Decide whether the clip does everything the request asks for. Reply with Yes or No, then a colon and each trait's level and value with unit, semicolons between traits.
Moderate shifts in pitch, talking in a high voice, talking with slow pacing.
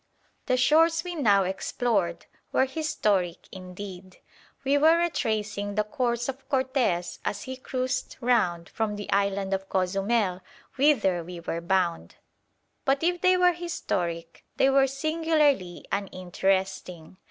No: wide, 6.5 semitones; high, 210 Hz; slow, 130 wpm